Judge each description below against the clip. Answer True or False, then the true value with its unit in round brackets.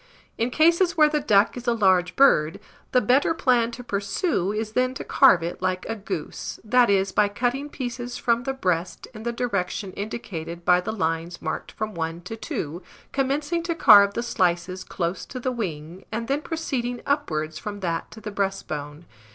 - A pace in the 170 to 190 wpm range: True (185 wpm)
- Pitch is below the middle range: False (210 Hz)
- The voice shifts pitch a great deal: True (5.8 semitones)